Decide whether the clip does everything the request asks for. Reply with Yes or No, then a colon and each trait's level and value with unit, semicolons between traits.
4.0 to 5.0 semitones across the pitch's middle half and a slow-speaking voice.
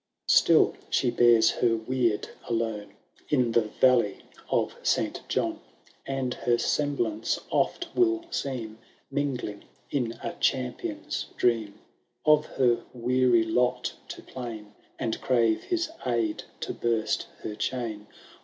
No: average, 2.7 semitones; slow, 125 wpm